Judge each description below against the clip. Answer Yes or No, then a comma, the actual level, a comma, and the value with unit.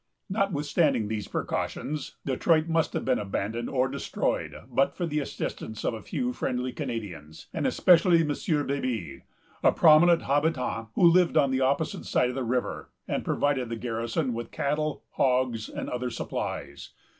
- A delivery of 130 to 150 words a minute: No, average, 160 wpm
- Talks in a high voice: No, low, 135 Hz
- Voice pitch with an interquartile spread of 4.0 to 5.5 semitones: Yes, average, 4.7 semitones